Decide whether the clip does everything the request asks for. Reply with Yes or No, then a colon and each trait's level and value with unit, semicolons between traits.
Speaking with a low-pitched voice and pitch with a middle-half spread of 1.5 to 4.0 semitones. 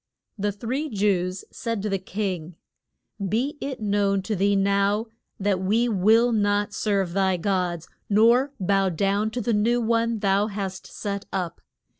No: high, 205 Hz; narrow, 2.5 semitones